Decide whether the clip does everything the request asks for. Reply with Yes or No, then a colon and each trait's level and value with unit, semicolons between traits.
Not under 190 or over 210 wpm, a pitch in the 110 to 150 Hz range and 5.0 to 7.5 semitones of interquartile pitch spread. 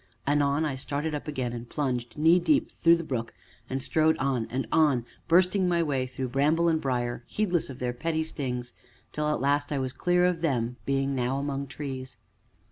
No: average, 195 wpm; medium, 140 Hz; average, 3.7 semitones